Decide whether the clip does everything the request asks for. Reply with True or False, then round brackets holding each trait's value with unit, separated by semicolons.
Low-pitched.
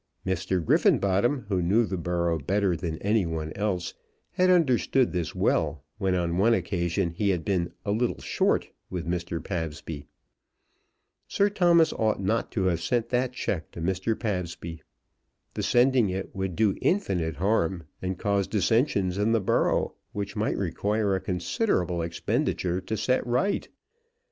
True (95 Hz)